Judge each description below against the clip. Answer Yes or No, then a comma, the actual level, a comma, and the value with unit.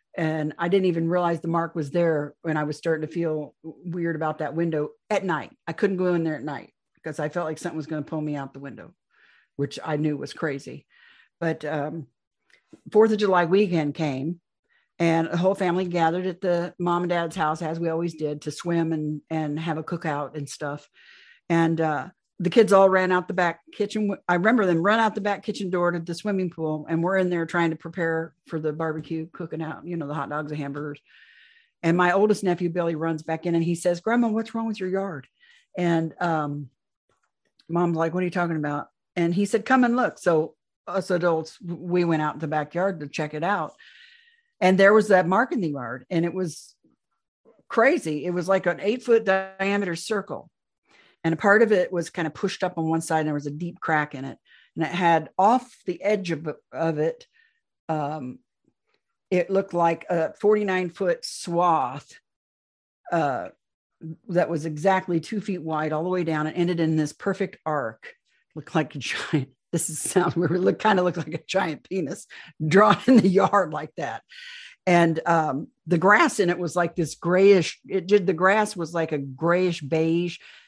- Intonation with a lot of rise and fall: No, average, 3.4 semitones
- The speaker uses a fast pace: Yes, fast, 210 wpm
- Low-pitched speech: No, medium, 170 Hz